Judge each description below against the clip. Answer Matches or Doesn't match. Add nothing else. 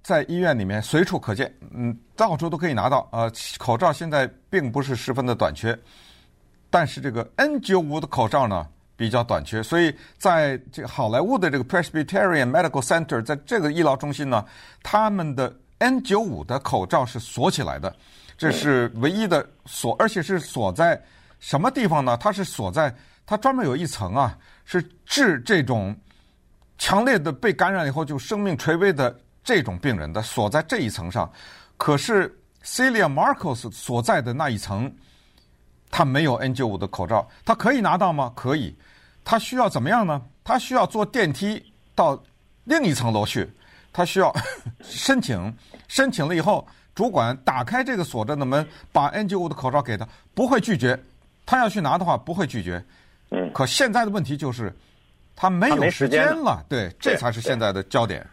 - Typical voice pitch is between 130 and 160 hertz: Matches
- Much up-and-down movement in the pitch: Matches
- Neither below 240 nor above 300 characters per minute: Matches